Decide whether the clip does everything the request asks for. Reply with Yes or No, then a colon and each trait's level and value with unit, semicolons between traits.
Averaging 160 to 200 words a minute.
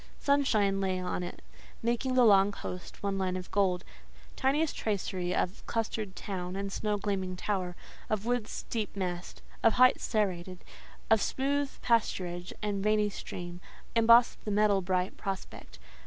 No: average, 145 wpm